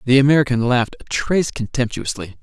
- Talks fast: No, average, 150 wpm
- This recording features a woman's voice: No, male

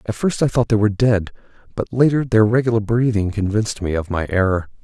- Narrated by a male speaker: Yes, male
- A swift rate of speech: Yes, fast, 210 wpm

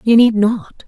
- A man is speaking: No, female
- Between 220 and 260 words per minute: No, fast, 205 wpm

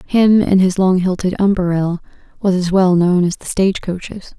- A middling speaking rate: Yes, average, 190 wpm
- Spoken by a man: No, female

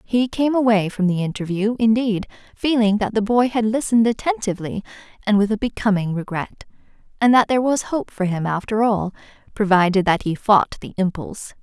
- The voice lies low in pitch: No, high, 210 Hz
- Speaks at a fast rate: No, average, 175 wpm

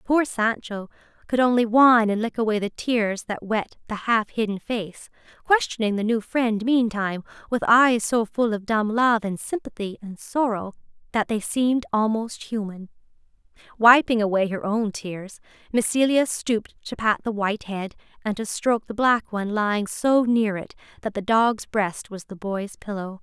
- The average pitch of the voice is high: Yes, high, 220 Hz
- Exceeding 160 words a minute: Yes, average, 175 wpm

